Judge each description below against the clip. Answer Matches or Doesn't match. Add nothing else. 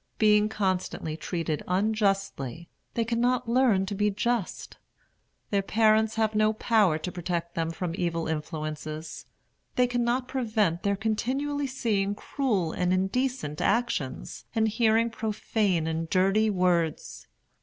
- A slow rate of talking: Matches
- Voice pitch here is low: Doesn't match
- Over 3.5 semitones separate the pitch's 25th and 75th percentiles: Matches